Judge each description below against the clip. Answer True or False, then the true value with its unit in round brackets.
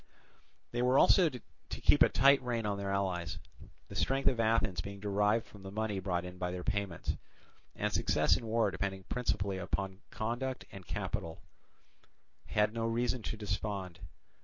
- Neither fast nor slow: True (160 wpm)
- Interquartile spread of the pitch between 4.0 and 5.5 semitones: False (3.3 semitones)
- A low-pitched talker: True (105 Hz)